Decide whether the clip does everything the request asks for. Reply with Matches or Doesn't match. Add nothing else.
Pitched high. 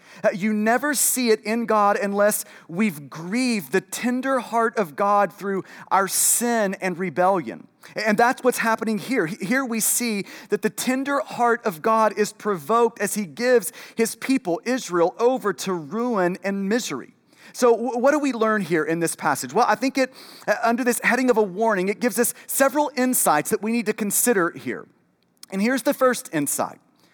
Matches